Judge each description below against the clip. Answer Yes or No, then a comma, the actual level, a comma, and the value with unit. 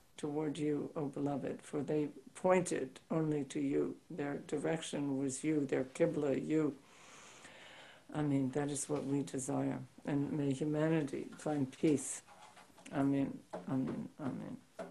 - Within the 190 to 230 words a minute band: No, average, 140 wpm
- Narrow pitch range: Yes, narrow, 2.0 semitones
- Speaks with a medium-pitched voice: Yes, medium, 145 Hz